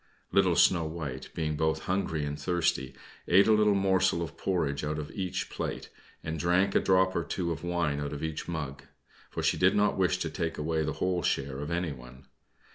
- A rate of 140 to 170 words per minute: No, average, 200 wpm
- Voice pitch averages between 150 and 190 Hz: No, very low, 80 Hz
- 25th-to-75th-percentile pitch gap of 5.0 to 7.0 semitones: No, average, 3.6 semitones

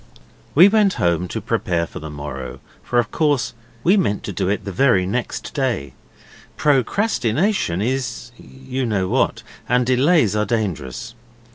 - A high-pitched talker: No, low, 120 Hz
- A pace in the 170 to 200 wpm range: No, average, 160 wpm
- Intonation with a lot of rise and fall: Yes, wide, 6.5 semitones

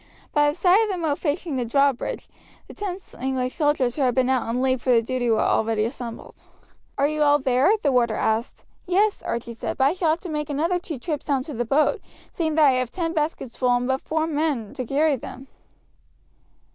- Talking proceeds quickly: Yes, fast, 220 wpm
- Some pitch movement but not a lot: Yes, average, 4.1 semitones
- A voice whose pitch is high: Yes, very high, 280 Hz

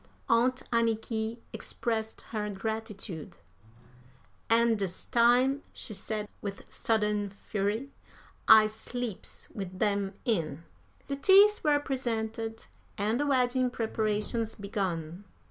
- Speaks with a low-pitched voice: No, high, 220 Hz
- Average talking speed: No, slow, 105 wpm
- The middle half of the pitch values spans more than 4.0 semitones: No, average, 2.7 semitones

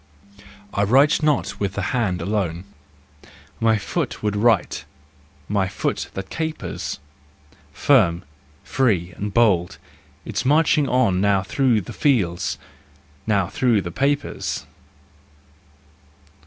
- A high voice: No, low, 105 Hz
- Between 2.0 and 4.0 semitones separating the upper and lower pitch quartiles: No, average, 5.2 semitones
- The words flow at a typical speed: No, slow, 110 wpm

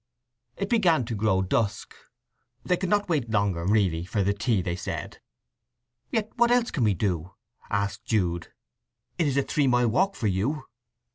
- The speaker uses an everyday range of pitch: No, wide, 8.5 semitones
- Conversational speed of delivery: Yes, average, 170 wpm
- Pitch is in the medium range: No, low, 110 Hz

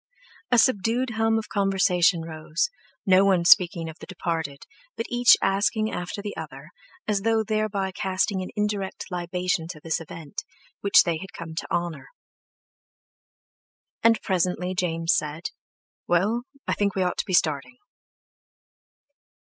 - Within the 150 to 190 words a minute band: No, average, 140 wpm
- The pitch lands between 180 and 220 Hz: Yes, medium, 185 Hz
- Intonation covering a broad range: No, average, 3.8 semitones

